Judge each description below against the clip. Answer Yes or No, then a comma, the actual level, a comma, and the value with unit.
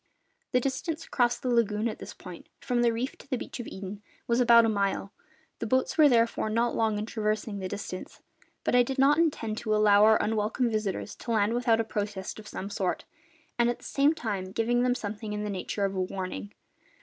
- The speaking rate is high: Yes, fast, 220 wpm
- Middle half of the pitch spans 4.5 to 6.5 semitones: No, average, 2.9 semitones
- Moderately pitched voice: No, high, 220 Hz